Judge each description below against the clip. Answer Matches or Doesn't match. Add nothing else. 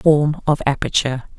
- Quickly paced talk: Doesn't match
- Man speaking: Doesn't match